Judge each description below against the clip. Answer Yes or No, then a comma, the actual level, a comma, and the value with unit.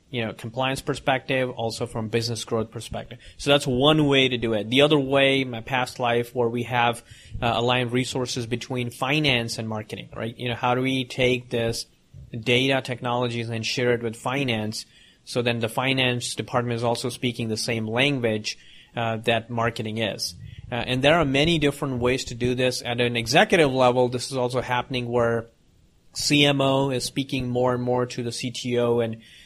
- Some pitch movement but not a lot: No, narrow, 1.8 semitones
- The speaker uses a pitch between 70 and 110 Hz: No, low, 125 Hz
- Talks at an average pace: Yes, average, 185 wpm